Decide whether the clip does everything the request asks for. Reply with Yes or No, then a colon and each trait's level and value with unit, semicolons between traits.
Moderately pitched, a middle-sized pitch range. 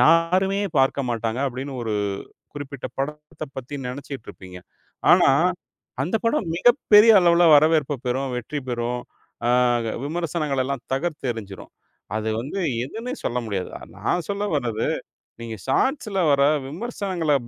No: medium, 145 Hz; wide, 6.0 semitones